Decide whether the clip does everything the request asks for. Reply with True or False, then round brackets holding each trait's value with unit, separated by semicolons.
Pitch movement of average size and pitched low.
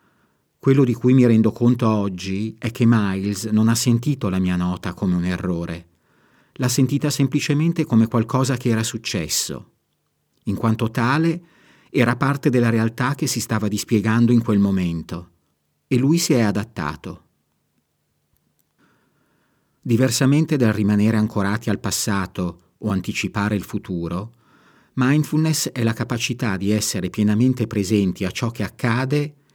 True (4.3 semitones; 110 Hz)